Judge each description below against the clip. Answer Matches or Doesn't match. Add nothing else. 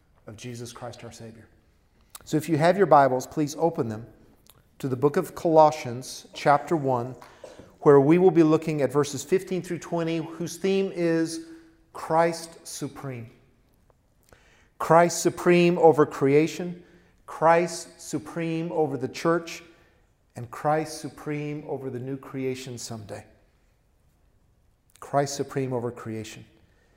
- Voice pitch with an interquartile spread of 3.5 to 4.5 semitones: Doesn't match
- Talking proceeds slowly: Matches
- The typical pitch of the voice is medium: Matches